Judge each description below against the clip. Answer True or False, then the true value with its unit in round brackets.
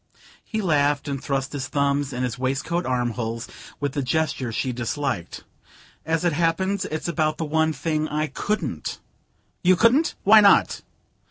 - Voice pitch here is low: False (145 Hz)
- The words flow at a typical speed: True (155 wpm)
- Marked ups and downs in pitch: False (4.0 semitones)